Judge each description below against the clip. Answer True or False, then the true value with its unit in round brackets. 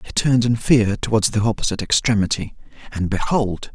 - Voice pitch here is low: True (110 Hz)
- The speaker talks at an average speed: True (145 wpm)